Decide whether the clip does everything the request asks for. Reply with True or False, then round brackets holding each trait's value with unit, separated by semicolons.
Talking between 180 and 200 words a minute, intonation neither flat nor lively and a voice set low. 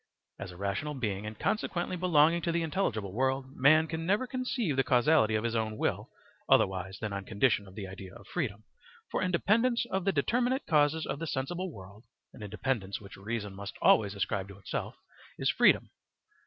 False (185 wpm; 8.8 semitones; 130 Hz)